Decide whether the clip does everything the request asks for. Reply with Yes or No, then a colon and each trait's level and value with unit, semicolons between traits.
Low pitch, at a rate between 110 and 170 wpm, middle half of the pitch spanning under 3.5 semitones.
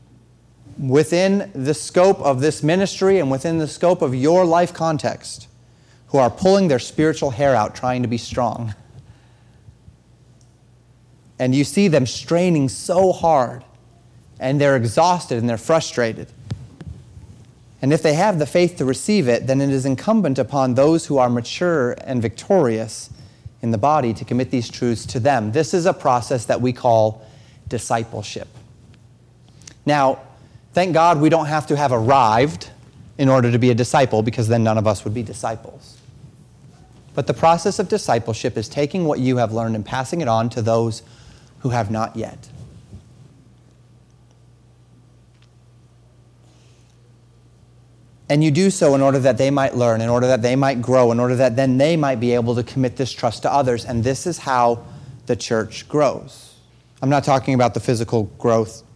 Yes: low, 125 Hz; average, 165 wpm; average, 3.1 semitones